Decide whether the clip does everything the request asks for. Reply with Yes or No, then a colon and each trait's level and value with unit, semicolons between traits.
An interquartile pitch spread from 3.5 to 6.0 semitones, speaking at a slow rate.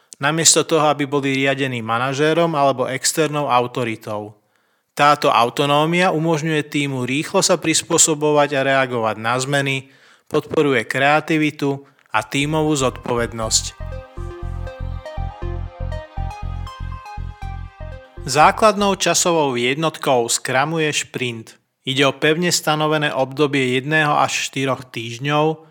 Yes: wide, 5.5 semitones; slow, 90 wpm